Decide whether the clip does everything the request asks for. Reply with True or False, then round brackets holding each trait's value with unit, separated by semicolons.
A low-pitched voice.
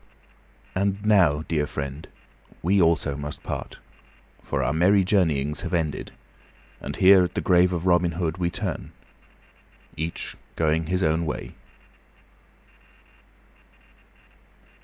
True (85 Hz)